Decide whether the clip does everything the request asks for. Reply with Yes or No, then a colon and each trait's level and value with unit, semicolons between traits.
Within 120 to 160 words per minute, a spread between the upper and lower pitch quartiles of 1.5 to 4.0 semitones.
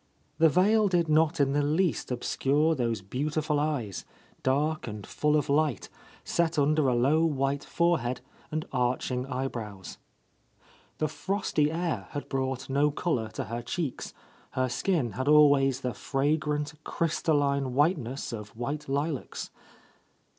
Yes: average, 145 wpm; average, 3.3 semitones